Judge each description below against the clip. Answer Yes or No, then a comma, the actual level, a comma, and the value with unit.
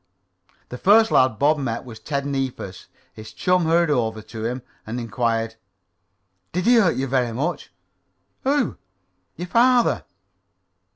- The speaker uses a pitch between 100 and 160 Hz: Yes, low, 135 Hz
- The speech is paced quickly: No, slow, 135 wpm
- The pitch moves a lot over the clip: Yes, wide, 7.4 semitones